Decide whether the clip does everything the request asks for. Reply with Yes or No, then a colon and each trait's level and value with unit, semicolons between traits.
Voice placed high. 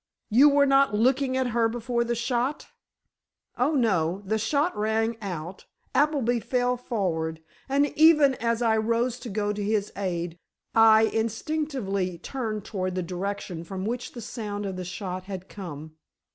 Yes: high, 220 Hz